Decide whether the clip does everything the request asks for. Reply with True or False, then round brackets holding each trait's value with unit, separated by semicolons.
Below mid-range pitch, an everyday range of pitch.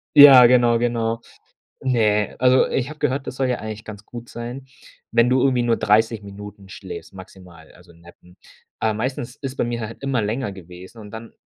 True (115 Hz; 3.5 semitones)